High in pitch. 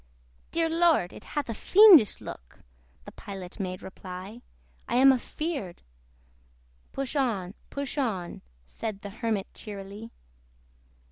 Yes: high, 220 Hz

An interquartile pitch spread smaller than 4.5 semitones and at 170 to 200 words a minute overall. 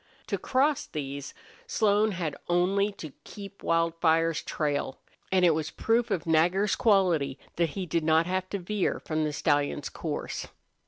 No: average, 4.1 semitones; average, 155 wpm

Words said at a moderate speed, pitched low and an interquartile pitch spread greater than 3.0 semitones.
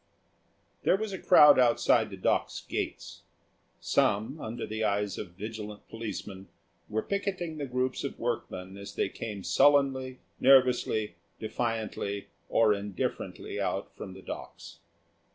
No: slow, 130 wpm; low, 110 Hz; average, 4.4 semitones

